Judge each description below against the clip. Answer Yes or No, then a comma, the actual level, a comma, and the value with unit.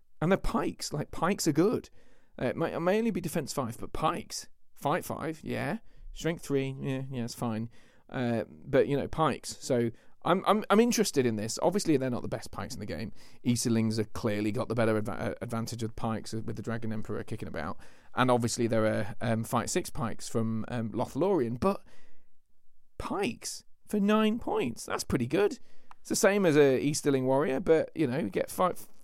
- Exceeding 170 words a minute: Yes, average, 200 wpm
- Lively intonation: Yes, wide, 6.3 semitones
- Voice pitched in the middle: No, low, 120 Hz